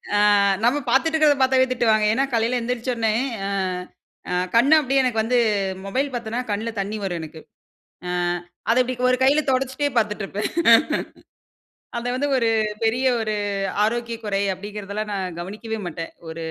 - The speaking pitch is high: Yes, high, 230 Hz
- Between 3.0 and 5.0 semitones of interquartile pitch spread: Yes, average, 3.6 semitones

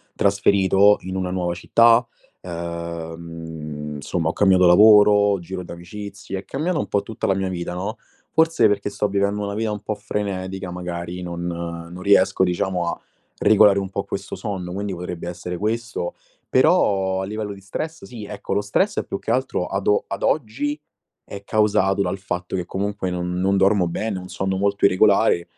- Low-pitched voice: Yes, very low, 95 Hz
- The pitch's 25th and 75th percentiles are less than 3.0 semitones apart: Yes, narrow, 2.6 semitones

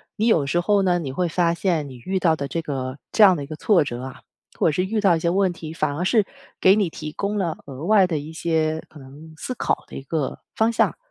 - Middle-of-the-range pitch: Yes, medium, 165 Hz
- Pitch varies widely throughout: No, average, 4.2 semitones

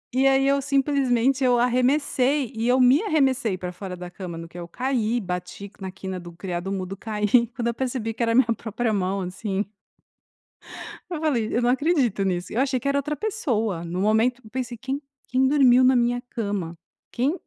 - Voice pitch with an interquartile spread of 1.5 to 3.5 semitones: No, wide, 5.4 semitones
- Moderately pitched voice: No, high, 240 Hz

